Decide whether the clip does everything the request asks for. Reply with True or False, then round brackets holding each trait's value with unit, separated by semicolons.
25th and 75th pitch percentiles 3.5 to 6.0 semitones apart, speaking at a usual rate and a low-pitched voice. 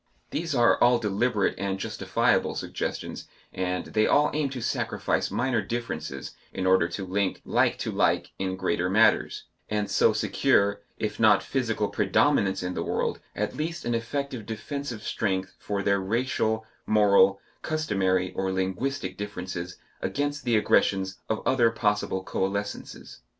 True (4.1 semitones; 145 wpm; 105 Hz)